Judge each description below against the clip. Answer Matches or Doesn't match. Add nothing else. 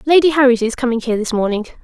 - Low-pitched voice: Doesn't match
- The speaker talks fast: Matches